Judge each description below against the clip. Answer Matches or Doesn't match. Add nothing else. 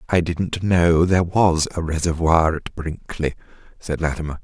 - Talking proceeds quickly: Doesn't match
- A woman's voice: Doesn't match